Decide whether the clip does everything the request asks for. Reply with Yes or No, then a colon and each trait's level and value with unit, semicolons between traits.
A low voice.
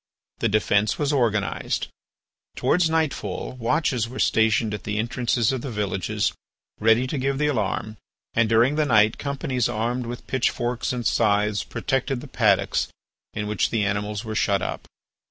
Yes: low, 115 Hz